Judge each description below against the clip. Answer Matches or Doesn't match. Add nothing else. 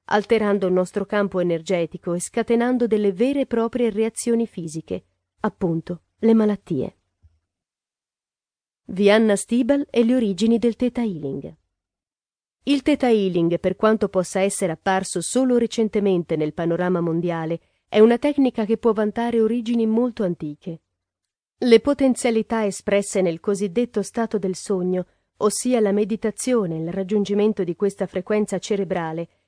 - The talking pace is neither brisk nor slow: Matches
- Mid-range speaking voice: Doesn't match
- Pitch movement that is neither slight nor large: Matches